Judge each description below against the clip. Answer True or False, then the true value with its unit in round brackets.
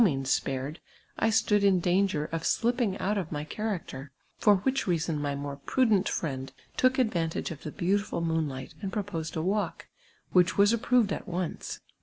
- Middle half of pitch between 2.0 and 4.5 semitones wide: False (5.3 semitones)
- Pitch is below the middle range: False (180 Hz)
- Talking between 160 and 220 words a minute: True (175 wpm)